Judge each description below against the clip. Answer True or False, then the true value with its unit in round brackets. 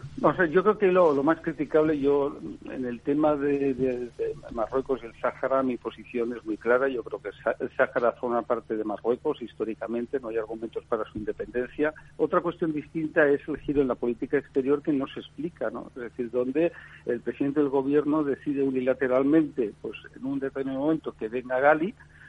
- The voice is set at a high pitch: False (135 Hz)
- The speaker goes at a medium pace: False (200 wpm)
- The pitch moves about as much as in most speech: True (3.7 semitones)